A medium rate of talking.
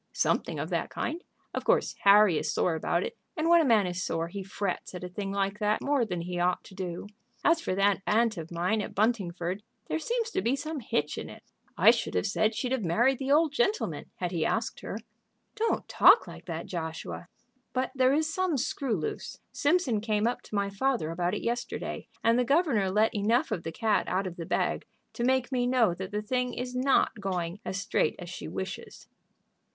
No: fast, 215 wpm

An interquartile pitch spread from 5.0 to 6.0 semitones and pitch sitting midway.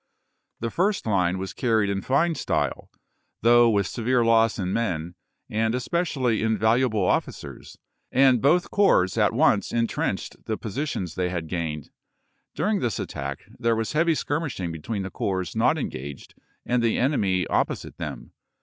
No: wide, 5.6 semitones; low, 110 Hz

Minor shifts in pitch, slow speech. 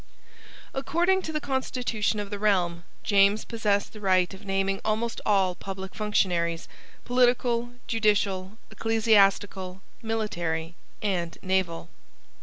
No: average, 3.1 semitones; slow, 110 wpm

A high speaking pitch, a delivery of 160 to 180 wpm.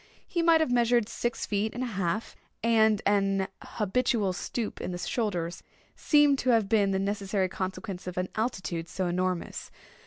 Yes: high, 205 Hz; average, 165 wpm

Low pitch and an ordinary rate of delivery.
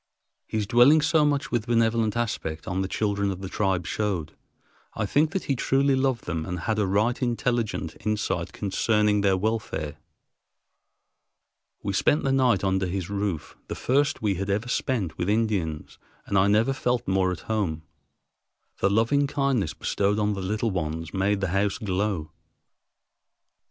Yes: low, 105 Hz; average, 160 wpm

